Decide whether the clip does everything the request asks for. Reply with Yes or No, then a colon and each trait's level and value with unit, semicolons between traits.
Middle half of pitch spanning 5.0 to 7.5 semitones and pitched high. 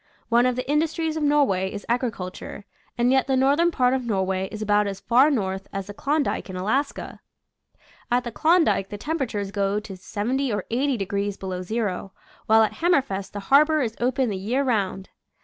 Yes: wide, 5.5 semitones; high, 230 Hz